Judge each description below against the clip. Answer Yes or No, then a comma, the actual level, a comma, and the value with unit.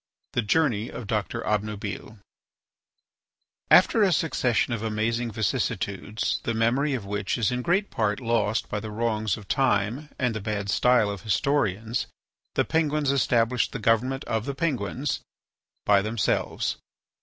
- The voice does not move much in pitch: No, average, 3.7 semitones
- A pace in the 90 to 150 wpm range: Yes, average, 145 wpm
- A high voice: No, low, 115 Hz